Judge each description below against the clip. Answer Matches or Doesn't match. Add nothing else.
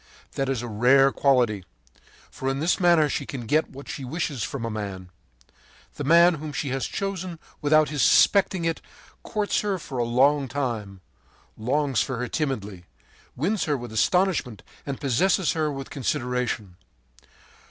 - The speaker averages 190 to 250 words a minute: Doesn't match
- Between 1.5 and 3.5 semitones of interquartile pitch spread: Doesn't match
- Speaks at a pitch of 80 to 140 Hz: Matches